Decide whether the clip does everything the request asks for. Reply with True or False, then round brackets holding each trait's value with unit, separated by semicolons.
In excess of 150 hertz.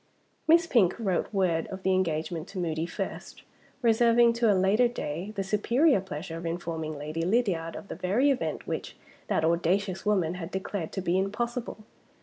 True (190 Hz)